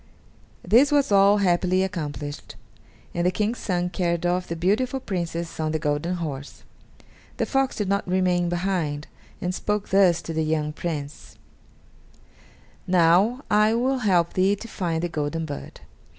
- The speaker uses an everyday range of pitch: Yes, average, 3.4 semitones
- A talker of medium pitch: Yes, medium, 180 Hz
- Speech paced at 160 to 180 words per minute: No, average, 150 wpm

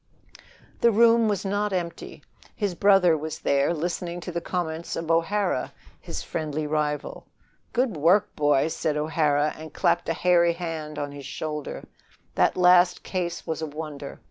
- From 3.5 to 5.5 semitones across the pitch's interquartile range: No, average, 3.0 semitones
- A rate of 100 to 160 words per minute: Yes, average, 155 wpm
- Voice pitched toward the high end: No, medium, 165 Hz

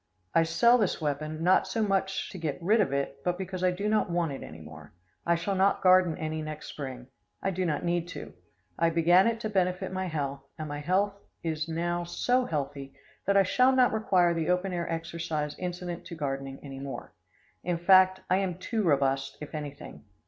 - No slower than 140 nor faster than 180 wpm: No, fast, 205 wpm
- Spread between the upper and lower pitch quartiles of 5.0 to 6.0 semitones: No, average, 3.9 semitones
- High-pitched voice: No, medium, 170 Hz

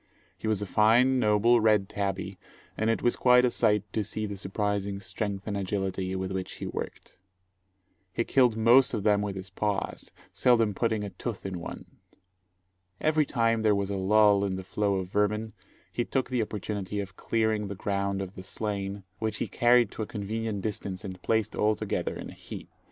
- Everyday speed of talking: Yes, average, 195 wpm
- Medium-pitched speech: No, low, 105 Hz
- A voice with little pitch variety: Yes, narrow, 2.3 semitones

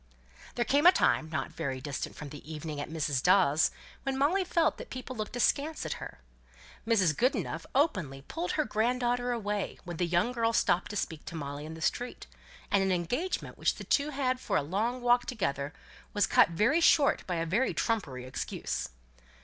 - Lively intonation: Yes, wide, 8.1 semitones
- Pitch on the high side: Yes, high, 205 Hz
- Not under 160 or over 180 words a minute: No, average, 200 wpm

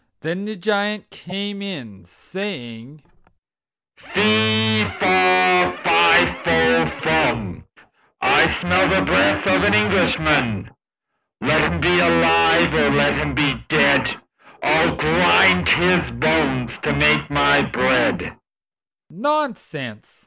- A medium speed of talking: No, slow, 105 wpm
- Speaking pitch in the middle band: No, low, 125 Hz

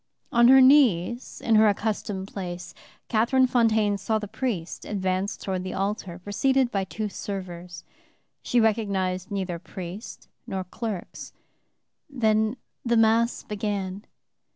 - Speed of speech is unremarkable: No, slow, 120 wpm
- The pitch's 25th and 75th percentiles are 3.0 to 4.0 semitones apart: Yes, average, 3.4 semitones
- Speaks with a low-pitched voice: No, high, 210 Hz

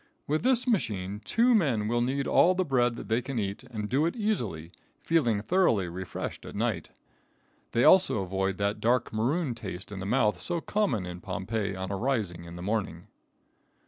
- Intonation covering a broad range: Yes, wide, 6.4 semitones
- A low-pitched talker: Yes, low, 110 Hz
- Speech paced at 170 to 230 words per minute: Yes, average, 175 wpm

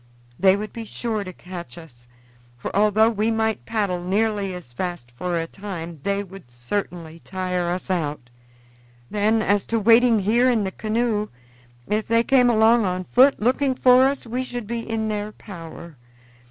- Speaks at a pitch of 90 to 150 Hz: No, high, 205 Hz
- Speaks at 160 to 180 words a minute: Yes, average, 170 wpm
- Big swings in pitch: No, average, 4.1 semitones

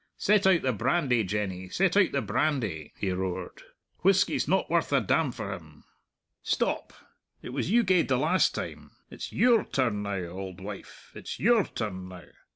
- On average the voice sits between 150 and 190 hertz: No, low, 120 Hz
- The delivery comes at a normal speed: Yes, average, 170 wpm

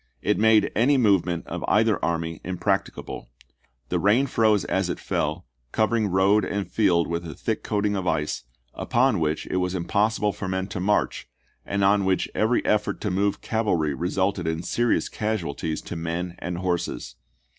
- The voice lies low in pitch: Yes, very low, 95 Hz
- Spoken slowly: No, average, 165 wpm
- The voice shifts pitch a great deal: No, average, 3.7 semitones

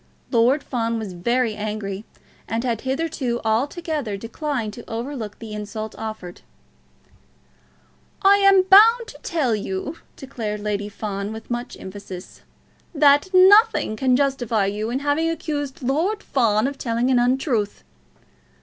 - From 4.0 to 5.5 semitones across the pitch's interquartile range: Yes, average, 5.2 semitones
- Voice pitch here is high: Yes, high, 240 Hz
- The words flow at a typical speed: No, slow, 130 wpm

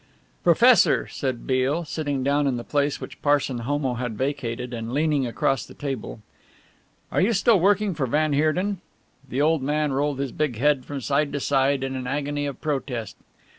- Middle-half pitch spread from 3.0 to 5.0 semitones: No, narrow, 2.4 semitones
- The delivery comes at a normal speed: Yes, average, 180 wpm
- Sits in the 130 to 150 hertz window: Yes, medium, 140 Hz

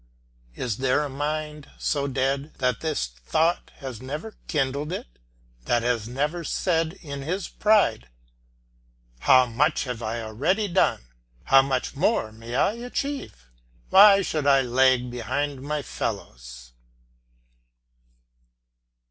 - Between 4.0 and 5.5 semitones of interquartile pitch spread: Yes, average, 4.3 semitones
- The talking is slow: Yes, slow, 120 wpm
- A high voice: No, low, 135 Hz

